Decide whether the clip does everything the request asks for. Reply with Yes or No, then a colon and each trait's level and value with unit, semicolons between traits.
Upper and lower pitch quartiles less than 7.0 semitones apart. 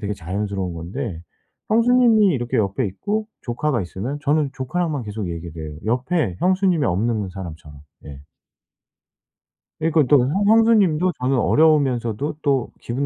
No: wide, 8.5 semitones